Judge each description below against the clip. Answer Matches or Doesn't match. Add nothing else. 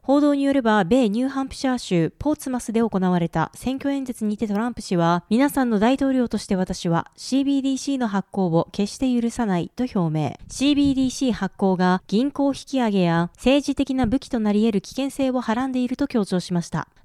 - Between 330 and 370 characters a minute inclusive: Doesn't match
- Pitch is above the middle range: Matches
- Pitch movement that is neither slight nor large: Doesn't match